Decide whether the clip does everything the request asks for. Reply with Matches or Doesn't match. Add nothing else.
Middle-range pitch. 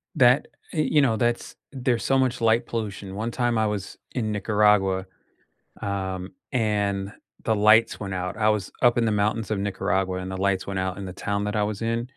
Doesn't match